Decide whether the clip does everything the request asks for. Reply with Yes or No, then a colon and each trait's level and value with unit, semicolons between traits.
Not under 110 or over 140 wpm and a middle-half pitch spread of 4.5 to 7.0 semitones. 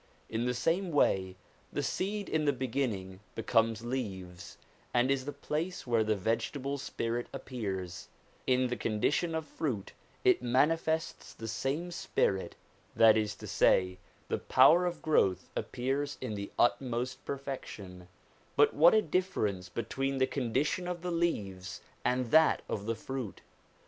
No: average, 150 wpm; wide, 5.6 semitones